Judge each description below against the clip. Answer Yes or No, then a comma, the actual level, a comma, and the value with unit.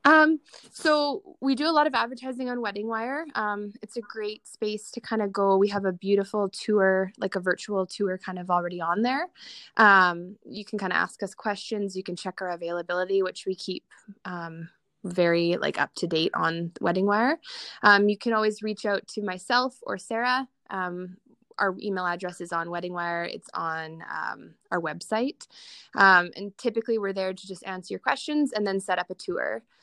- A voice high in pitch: Yes, high, 200 Hz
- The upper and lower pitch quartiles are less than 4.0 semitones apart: Yes, average, 3.5 semitones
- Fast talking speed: No, average, 190 wpm